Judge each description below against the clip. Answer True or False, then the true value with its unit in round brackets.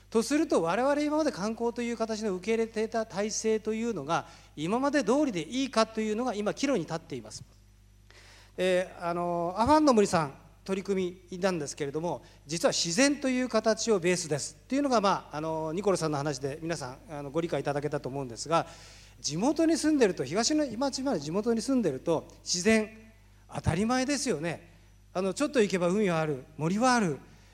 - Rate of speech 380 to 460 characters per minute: True (390 characters per minute)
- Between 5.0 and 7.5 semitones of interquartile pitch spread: False (7.9 semitones)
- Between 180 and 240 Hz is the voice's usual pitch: True (185 Hz)